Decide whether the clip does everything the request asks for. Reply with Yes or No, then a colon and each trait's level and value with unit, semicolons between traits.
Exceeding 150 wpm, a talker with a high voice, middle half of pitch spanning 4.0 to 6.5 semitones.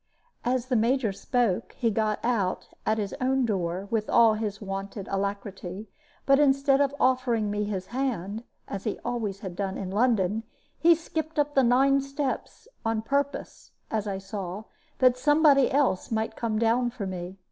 Yes: average, 170 wpm; high, 225 Hz; average, 4.7 semitones